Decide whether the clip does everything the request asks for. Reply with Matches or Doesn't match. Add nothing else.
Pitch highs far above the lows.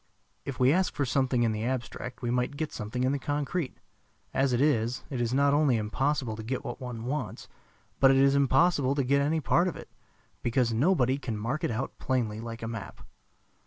Doesn't match